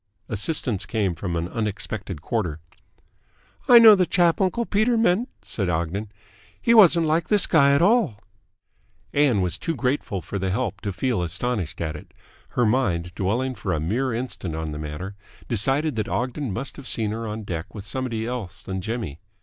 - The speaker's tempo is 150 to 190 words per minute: Yes, average, 180 wpm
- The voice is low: Yes, low, 110 Hz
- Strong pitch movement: Yes, wide, 6.9 semitones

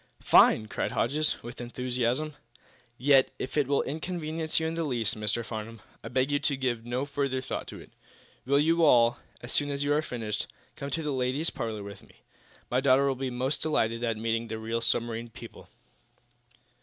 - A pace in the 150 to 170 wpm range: No, average, 190 wpm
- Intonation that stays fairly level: No, average, 3.7 semitones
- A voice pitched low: Yes, low, 130 Hz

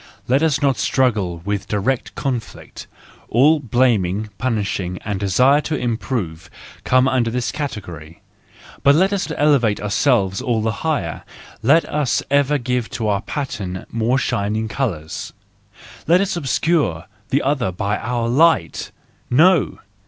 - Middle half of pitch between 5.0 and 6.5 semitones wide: Yes, wide, 5.6 semitones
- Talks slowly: Yes, slow, 130 wpm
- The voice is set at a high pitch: No, low, 120 Hz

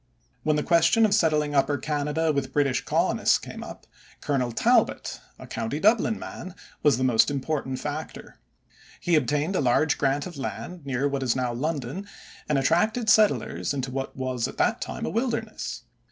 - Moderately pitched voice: Yes, medium, 145 Hz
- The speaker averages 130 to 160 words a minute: No, average, 170 wpm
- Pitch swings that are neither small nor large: Yes, average, 4.2 semitones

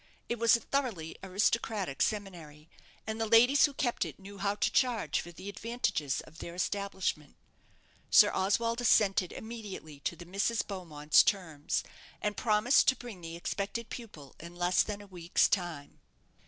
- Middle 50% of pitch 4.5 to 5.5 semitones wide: Yes, average, 4.8 semitones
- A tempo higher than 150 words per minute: Yes, average, 160 wpm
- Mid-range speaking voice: No, high, 200 Hz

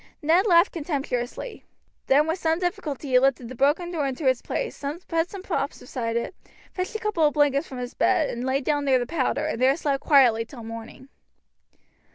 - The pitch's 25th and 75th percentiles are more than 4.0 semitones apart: Yes, average, 4.4 semitones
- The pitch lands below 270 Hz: No, very high, 285 Hz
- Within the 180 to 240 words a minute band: Yes, average, 200 wpm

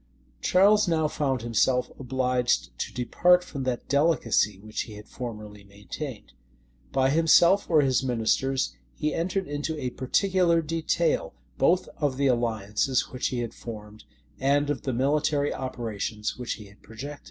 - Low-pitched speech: Yes, low, 130 Hz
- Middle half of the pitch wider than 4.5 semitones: Yes, average, 5.0 semitones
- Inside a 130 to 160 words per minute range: Yes, average, 150 wpm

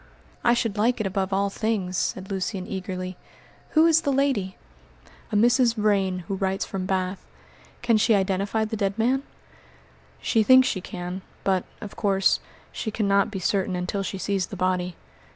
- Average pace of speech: Yes, average, 170 wpm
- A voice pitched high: Yes, high, 195 Hz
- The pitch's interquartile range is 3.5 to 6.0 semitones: No, average, 2.9 semitones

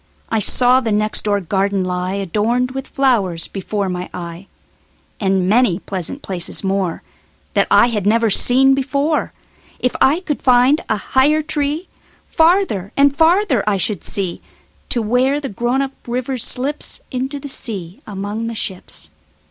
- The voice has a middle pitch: No, high, 230 Hz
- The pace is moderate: No, slow, 130 wpm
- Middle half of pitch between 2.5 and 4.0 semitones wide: No, wide, 5.6 semitones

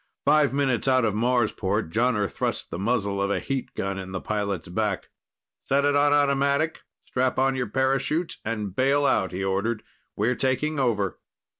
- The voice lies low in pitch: Yes, low, 125 Hz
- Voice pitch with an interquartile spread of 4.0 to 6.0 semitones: Yes, average, 5.3 semitones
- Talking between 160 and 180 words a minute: Yes, average, 170 wpm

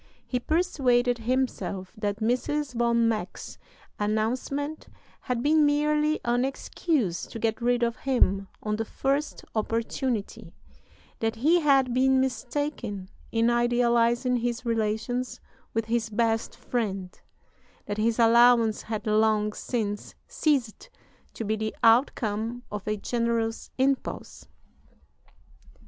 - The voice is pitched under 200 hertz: No, high, 235 Hz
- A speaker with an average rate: No, slow, 115 wpm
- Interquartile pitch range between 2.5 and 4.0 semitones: Yes, average, 2.8 semitones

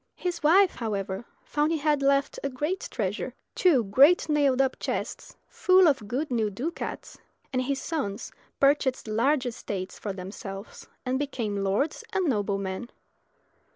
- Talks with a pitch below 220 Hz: No, very high, 260 Hz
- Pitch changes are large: Yes, wide, 6.3 semitones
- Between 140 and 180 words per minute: Yes, average, 145 wpm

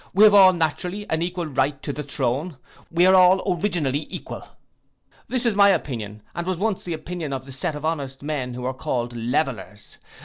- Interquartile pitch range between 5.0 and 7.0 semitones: Yes, wide, 5.5 semitones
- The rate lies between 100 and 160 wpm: No, average, 200 wpm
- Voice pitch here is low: No, medium, 155 Hz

